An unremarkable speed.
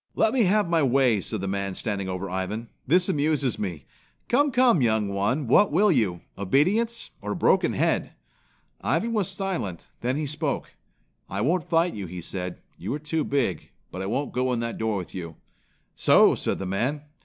Yes: average, 190 wpm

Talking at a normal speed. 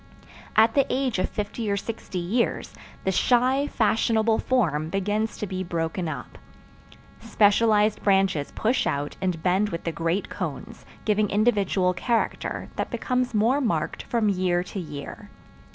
Yes: average, 145 wpm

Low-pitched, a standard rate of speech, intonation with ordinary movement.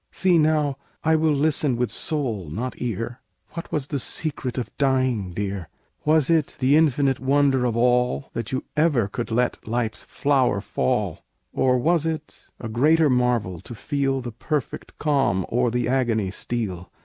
Yes: low, 130 Hz; average, 160 wpm; average, 3.9 semitones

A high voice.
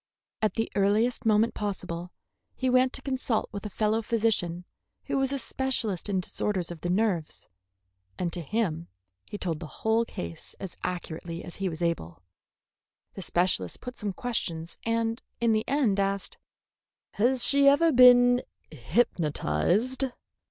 Yes: high, 210 Hz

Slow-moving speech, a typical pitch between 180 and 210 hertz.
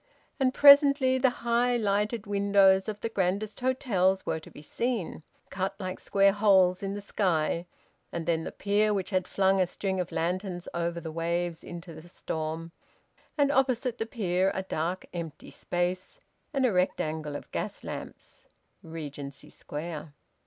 No: average, 160 wpm; high, 190 Hz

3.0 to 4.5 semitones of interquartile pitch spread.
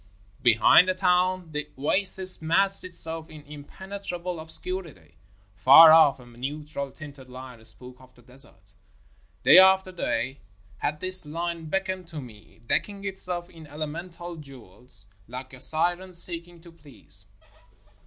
No: average, 5.3 semitones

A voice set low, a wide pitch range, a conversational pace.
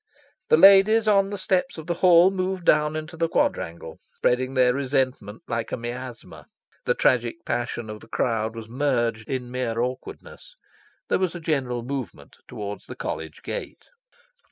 Yes: low, 130 Hz; wide, 6.6 semitones; average, 160 wpm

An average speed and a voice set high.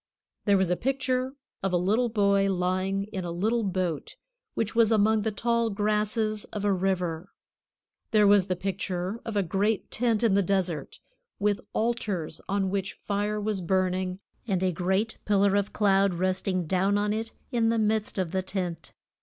Yes: average, 175 wpm; high, 200 Hz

